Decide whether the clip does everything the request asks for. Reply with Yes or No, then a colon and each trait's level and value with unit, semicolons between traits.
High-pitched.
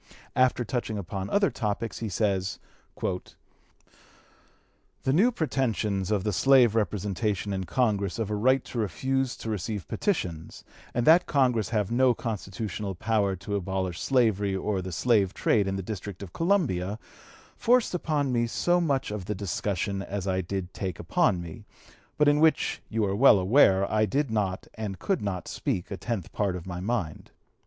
No: low, 105 Hz